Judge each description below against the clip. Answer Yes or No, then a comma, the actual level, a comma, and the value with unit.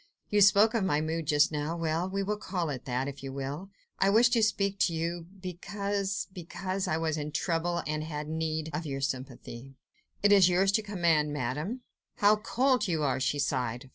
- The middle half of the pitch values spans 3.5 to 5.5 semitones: Yes, average, 5.0 semitones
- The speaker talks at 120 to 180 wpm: No, average, 200 wpm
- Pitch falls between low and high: Yes, medium, 165 Hz